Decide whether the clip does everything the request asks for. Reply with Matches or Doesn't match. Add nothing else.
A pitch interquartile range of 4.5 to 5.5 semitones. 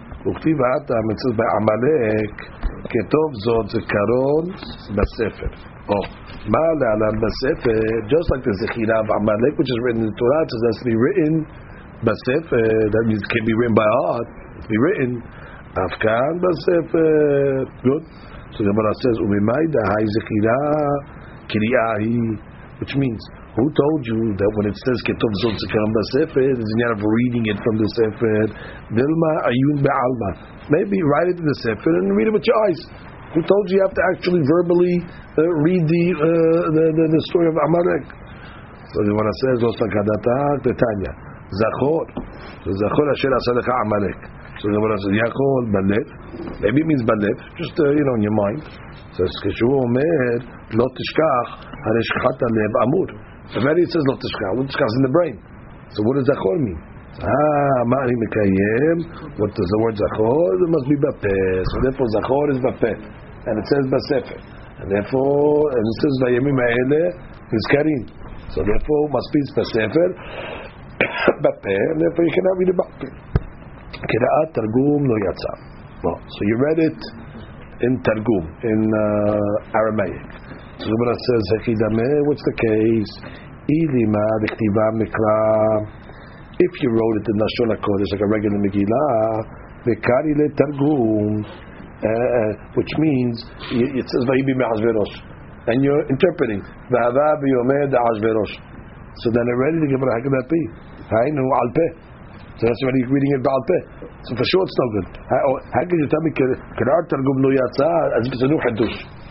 Matches